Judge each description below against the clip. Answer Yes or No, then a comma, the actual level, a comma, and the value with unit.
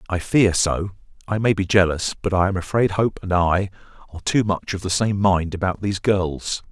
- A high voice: No, very low, 95 Hz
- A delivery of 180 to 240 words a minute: Yes, average, 195 wpm